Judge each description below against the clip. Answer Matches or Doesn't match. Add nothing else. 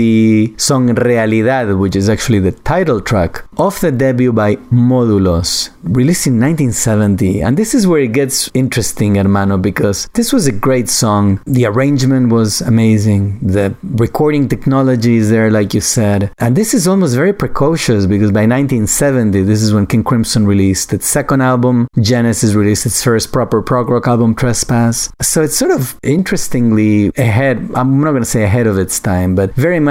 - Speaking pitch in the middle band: Doesn't match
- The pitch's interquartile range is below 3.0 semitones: Doesn't match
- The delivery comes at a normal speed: Matches